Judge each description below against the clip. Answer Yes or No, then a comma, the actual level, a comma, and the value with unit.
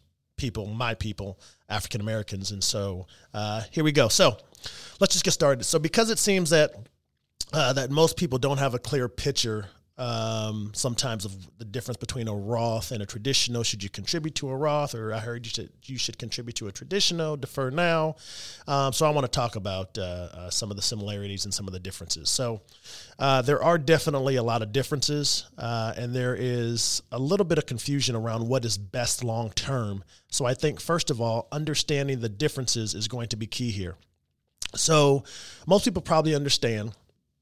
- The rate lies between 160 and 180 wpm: No, average, 195 wpm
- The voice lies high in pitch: No, low, 120 Hz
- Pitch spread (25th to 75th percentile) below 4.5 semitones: No, average, 5.1 semitones